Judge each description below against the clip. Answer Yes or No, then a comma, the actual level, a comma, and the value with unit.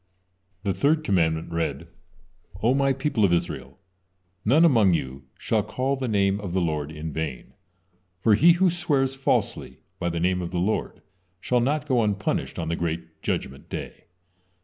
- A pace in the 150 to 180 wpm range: Yes, average, 170 wpm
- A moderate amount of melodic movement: No, wide, 8.2 semitones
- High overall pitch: No, low, 100 Hz